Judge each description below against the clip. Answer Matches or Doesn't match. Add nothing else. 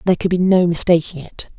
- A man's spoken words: Doesn't match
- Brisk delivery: Matches